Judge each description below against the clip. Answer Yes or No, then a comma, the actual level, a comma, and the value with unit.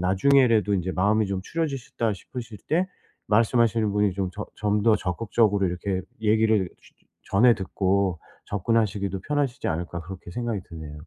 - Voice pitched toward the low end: Yes, low, 105 Hz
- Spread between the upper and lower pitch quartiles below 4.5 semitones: Yes, average, 3.5 semitones